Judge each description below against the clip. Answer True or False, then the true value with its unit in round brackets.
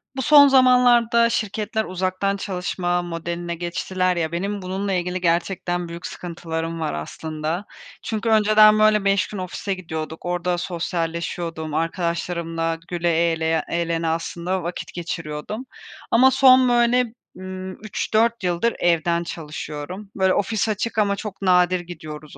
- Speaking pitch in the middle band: True (180 Hz)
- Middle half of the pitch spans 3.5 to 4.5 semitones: True (3.9 semitones)